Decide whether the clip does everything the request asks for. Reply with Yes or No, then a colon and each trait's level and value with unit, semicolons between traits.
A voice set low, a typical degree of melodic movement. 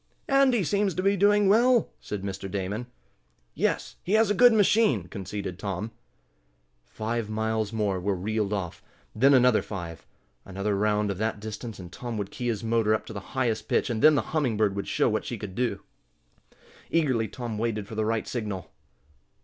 Yes: low, 110 Hz; average, 4.5 semitones